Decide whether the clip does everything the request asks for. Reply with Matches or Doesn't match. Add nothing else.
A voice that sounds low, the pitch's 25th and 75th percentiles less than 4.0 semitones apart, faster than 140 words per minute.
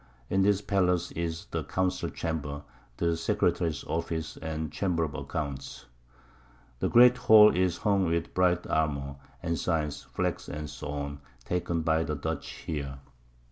Doesn't match